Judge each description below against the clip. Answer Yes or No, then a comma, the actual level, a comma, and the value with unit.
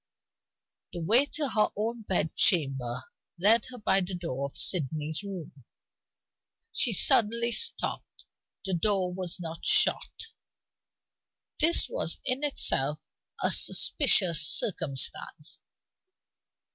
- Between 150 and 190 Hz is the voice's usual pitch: Yes, medium, 185 Hz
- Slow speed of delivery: Yes, slow, 105 wpm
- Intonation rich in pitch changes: Yes, wide, 6.7 semitones